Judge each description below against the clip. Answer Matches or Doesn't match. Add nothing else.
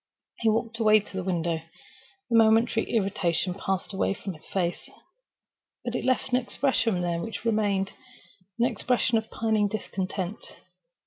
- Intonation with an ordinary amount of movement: Matches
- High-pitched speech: Matches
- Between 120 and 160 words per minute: Matches